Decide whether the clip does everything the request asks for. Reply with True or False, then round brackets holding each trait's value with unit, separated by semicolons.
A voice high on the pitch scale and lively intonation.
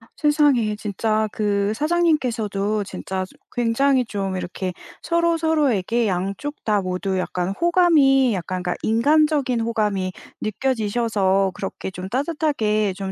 True (220 Hz; 6.3 semitones)